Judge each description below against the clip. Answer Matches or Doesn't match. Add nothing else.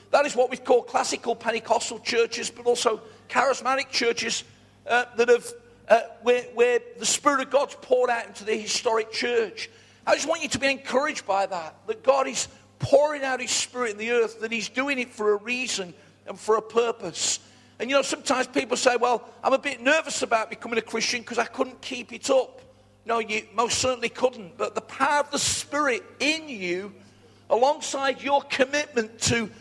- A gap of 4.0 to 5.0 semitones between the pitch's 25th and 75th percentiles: Doesn't match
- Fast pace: Doesn't match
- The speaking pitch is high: Matches